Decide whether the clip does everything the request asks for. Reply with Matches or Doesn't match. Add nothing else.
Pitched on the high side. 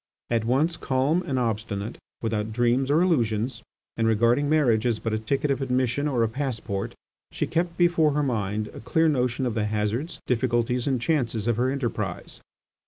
Doesn't match